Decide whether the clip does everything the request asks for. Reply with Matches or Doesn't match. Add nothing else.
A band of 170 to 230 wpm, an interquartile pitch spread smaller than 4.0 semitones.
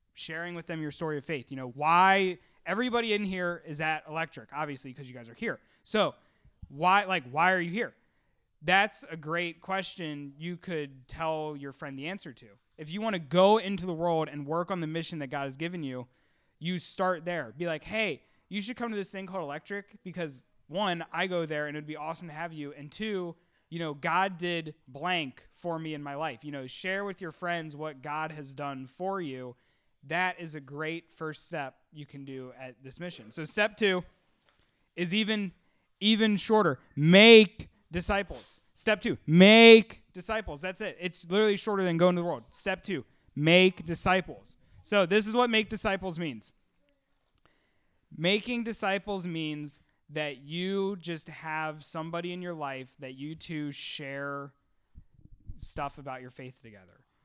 Doesn't match